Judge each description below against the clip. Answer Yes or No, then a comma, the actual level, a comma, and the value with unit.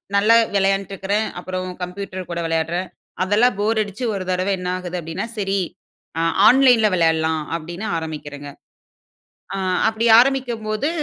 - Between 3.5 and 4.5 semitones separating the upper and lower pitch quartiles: Yes, average, 4.2 semitones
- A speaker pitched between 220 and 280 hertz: No, high, 195 Hz